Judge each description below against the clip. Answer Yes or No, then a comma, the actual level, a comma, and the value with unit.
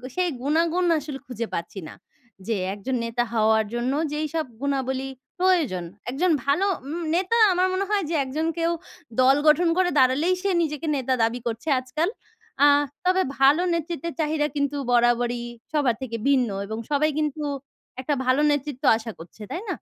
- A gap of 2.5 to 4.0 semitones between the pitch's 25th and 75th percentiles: No, average, 5.2 semitones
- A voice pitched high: Yes, very high, 285 Hz